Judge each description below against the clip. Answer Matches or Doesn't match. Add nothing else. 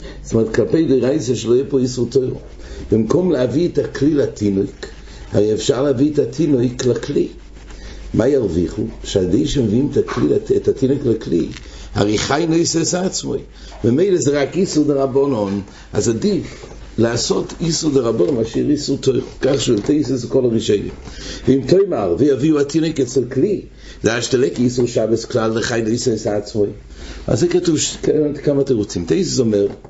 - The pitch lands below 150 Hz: Matches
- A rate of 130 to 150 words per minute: Matches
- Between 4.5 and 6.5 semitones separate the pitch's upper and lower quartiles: Matches